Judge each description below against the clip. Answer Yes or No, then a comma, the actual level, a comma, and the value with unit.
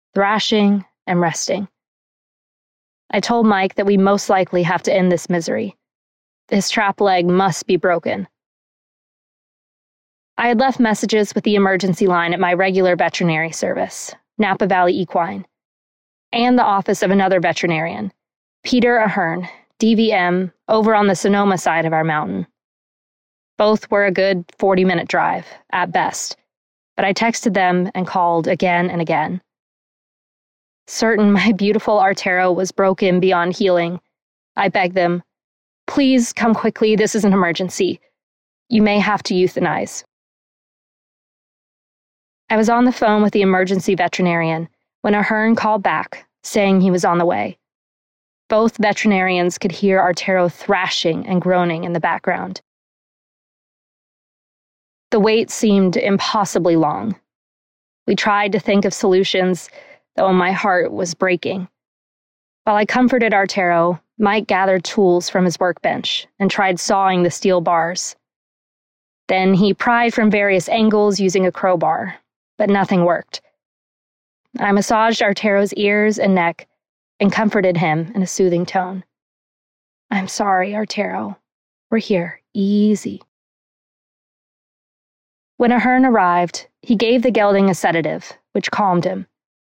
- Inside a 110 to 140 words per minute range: Yes, slow, 135 wpm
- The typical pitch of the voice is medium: No, high, 195 Hz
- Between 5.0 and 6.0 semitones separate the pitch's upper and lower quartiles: No, average, 2.8 semitones